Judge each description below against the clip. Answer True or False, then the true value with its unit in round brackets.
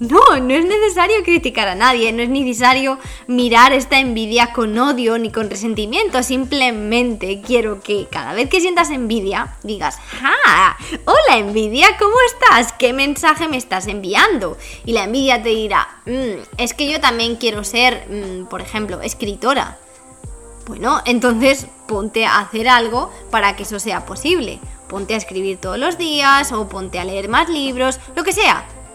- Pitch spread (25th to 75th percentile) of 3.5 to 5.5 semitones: True (4.1 semitones)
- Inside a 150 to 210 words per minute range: True (165 wpm)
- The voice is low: False (245 Hz)